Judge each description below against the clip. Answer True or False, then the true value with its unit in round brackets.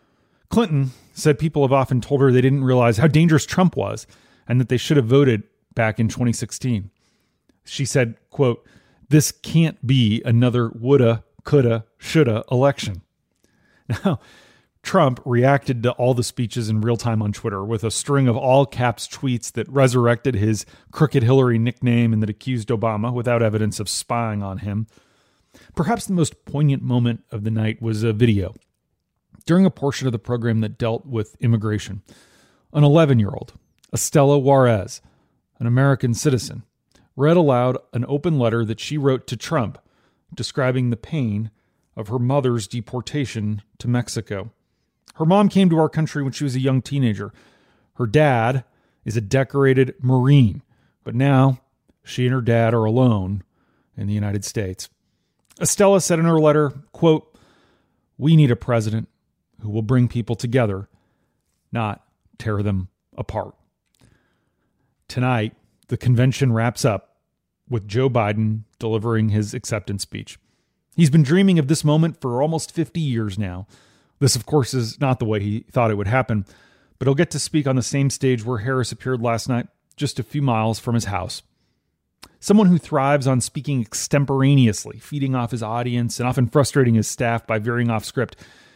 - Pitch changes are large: False (3.7 semitones)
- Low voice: True (125 Hz)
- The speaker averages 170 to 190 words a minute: False (160 wpm)